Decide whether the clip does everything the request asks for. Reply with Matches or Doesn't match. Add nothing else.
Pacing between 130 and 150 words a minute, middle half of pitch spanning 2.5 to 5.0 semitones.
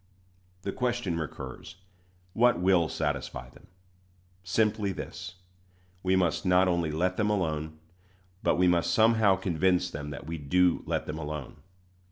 Matches